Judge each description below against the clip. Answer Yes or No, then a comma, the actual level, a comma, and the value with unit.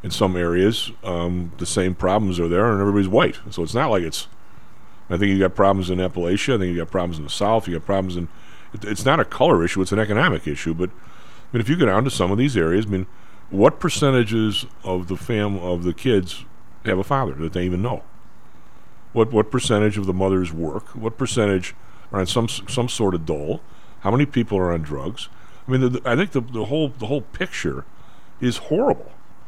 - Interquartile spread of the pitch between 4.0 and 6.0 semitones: Yes, average, 4.6 semitones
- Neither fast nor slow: No, fast, 225 wpm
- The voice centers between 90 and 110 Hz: Yes, low, 100 Hz